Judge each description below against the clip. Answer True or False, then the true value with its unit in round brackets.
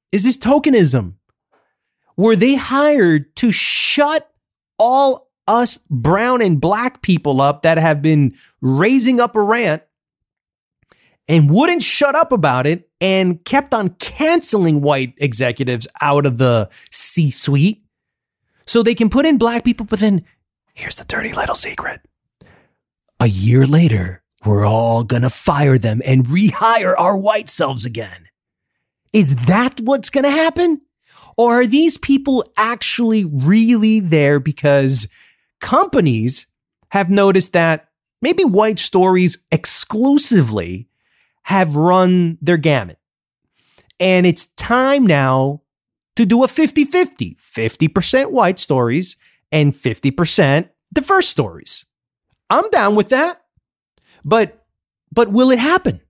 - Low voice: False (185 Hz)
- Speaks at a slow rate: True (125 wpm)